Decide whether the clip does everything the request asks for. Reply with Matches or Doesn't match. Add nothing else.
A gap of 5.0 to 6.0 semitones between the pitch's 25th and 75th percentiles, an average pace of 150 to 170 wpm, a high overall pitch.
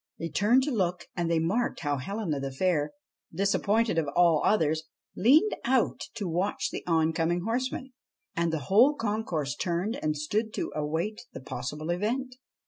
Doesn't match